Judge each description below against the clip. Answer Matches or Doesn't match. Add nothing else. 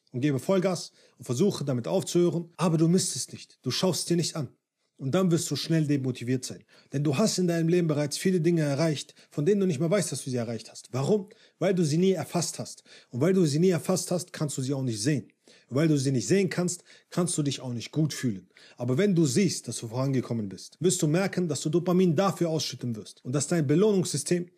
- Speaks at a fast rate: Matches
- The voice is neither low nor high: Matches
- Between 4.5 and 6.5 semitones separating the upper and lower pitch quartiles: Matches